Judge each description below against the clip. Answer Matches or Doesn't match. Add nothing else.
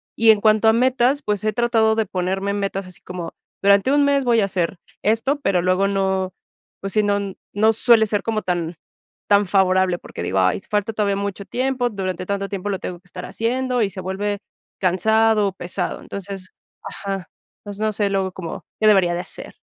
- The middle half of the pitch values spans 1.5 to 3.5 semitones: Matches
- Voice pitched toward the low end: Doesn't match